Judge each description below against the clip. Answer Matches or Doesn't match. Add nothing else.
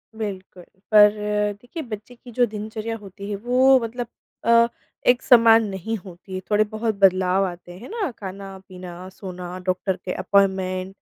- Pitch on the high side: Matches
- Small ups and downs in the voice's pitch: Doesn't match